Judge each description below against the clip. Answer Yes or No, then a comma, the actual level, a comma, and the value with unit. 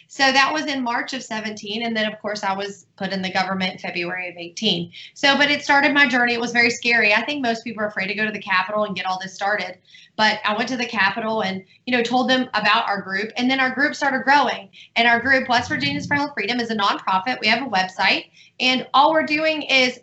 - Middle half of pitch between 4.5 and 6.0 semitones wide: Yes, average, 4.8 semitones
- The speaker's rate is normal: No, fast, 260 wpm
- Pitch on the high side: Yes, high, 225 Hz